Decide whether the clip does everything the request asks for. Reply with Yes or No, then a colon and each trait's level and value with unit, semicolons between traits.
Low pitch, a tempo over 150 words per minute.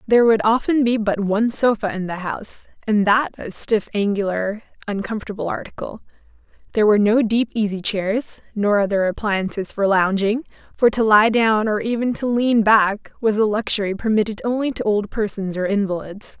No: high, 210 Hz; average, 170 wpm